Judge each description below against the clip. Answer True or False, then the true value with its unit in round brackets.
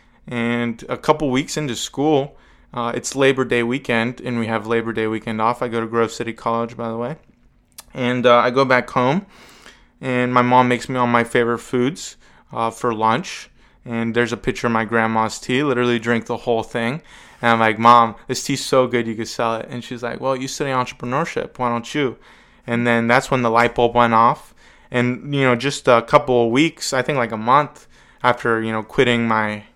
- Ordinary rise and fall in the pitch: False (1.5 semitones)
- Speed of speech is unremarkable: False (215 wpm)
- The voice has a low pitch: True (120 Hz)